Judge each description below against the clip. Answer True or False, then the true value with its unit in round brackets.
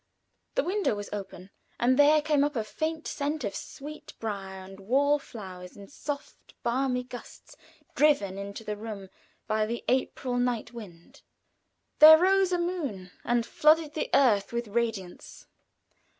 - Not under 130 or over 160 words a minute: True (145 wpm)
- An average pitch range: False (6.5 semitones)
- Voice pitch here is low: False (240 Hz)